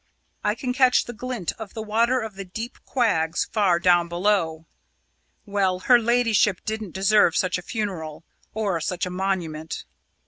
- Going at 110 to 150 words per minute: No, average, 160 wpm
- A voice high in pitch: Yes, high, 200 Hz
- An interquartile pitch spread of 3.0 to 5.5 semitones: Yes, average, 4.0 semitones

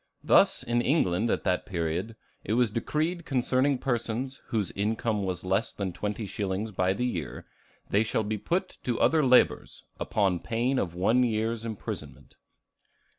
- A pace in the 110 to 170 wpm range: Yes, average, 155 wpm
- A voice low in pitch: Yes, low, 110 Hz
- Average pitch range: Yes, average, 4.2 semitones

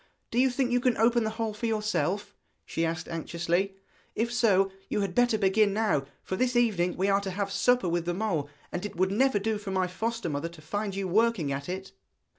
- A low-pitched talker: No, high, 200 Hz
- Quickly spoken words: Yes, fast, 225 wpm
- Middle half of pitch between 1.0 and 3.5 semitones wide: No, average, 4.1 semitones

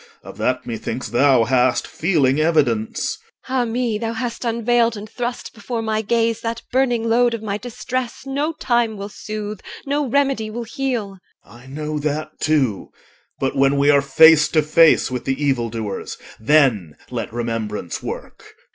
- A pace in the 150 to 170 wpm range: Yes, average, 165 wpm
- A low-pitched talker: No, high, 195 Hz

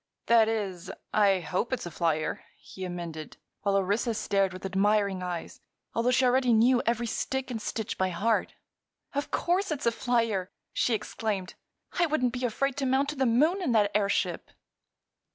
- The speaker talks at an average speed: Yes, average, 170 wpm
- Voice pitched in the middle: No, high, 225 Hz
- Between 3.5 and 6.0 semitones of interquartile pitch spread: Yes, average, 4.8 semitones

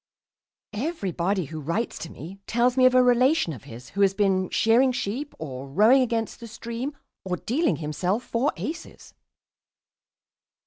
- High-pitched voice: Yes, high, 220 Hz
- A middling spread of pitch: No, wide, 5.8 semitones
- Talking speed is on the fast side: No, average, 150 wpm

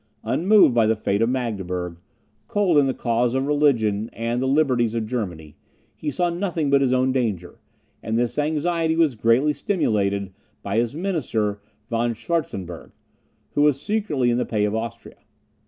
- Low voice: Yes, low, 120 Hz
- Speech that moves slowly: No, average, 165 wpm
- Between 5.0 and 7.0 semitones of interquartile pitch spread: Yes, average, 5.3 semitones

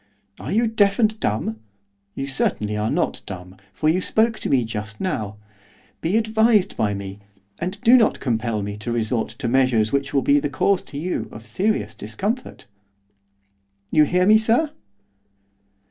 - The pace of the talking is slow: No, average, 165 wpm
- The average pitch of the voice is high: No, medium, 140 Hz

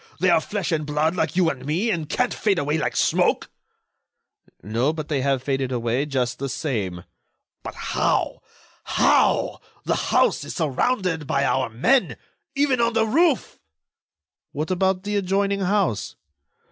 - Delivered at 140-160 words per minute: Yes, average, 150 wpm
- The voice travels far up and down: Yes, wide, 6.5 semitones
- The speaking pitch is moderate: Yes, medium, 160 Hz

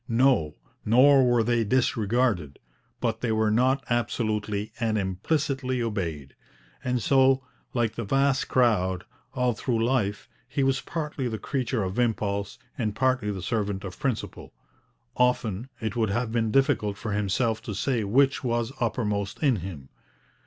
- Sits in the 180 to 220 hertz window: No, low, 115 Hz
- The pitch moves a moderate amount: Yes, average, 3.8 semitones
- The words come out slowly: No, average, 145 wpm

